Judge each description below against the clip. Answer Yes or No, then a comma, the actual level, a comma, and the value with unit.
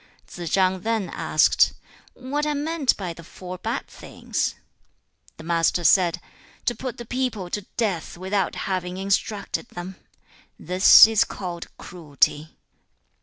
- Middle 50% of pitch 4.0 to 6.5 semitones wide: Yes, average, 4.3 semitones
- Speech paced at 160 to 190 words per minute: No, slow, 135 wpm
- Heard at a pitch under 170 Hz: No, high, 190 Hz